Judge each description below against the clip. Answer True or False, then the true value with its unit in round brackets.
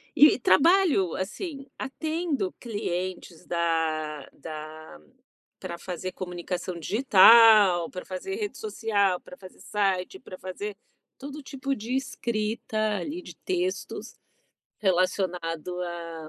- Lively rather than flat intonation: True (7.2 semitones)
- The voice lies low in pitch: False (190 Hz)